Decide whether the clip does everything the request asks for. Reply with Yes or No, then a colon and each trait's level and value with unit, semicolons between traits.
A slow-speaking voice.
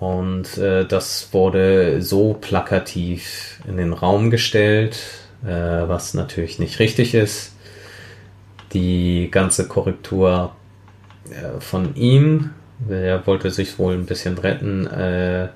Yes: slow, 115 wpm